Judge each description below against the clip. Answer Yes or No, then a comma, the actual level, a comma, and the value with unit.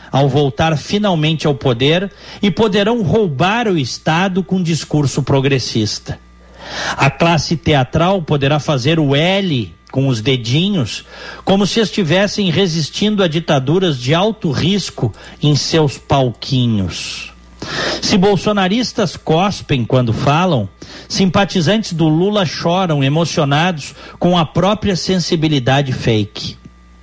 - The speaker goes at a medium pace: No, slow, 110 wpm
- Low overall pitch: No, medium, 160 Hz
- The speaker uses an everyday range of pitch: No, wide, 5.9 semitones